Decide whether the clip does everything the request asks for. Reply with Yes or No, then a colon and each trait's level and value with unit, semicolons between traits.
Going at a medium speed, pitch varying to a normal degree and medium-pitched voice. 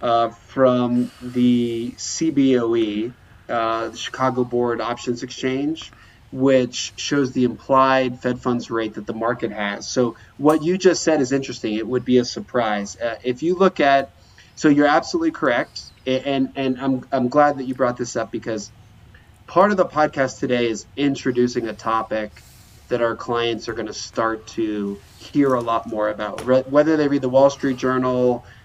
No: average, 175 wpm; average, 3.0 semitones; low, 125 Hz